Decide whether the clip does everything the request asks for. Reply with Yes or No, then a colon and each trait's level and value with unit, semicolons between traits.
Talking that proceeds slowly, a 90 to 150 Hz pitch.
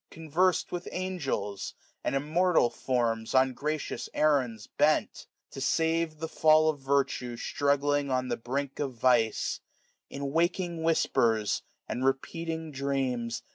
Yes: slow, 130 wpm; medium, 140 Hz